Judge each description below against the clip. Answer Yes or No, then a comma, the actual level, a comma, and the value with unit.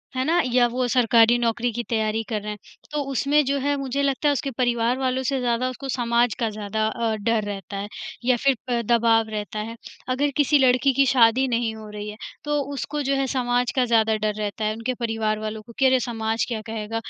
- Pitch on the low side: No, high, 235 Hz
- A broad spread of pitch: No, average, 2.9 semitones